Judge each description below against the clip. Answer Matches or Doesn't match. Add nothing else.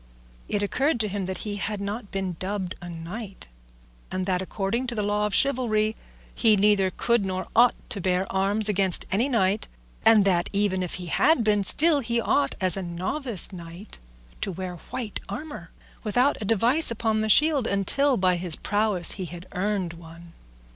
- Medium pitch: Doesn't match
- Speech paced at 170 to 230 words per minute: Matches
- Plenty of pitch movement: Doesn't match